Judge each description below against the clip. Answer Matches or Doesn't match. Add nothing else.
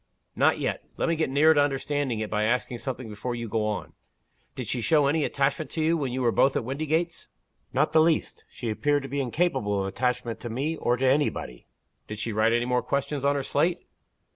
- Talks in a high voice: Doesn't match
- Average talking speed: Doesn't match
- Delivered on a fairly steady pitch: Doesn't match